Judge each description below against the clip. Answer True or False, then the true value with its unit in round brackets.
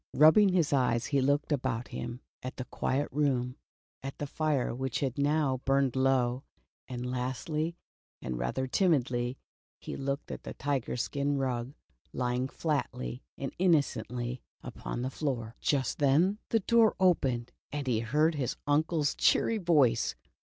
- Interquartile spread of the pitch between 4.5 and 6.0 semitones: False (3.2 semitones)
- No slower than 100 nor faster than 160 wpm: True (150 wpm)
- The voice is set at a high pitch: False (135 Hz)